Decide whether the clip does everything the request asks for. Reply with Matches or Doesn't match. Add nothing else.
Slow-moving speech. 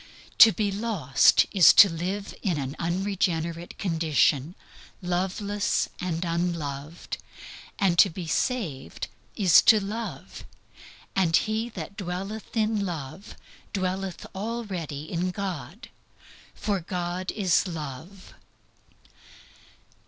Matches